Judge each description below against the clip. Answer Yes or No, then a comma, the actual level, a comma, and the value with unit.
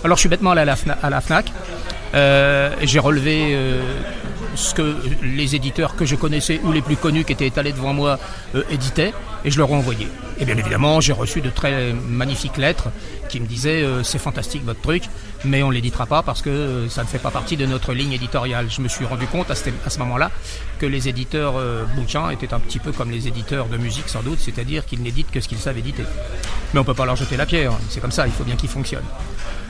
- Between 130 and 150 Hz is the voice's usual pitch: Yes, low, 135 Hz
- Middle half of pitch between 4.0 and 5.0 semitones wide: No, average, 3.0 semitones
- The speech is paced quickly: Yes, fast, 235 wpm